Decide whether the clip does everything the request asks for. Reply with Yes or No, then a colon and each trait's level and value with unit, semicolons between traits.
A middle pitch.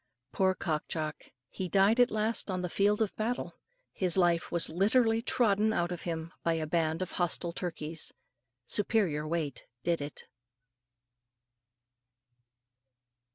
Yes: medium, 180 Hz